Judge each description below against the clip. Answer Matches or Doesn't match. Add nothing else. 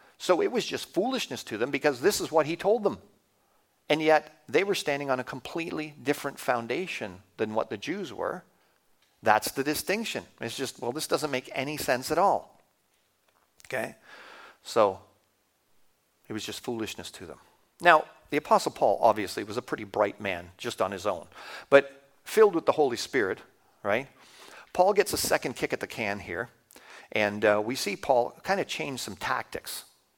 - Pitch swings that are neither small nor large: Doesn't match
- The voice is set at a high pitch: Doesn't match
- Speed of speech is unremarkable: Matches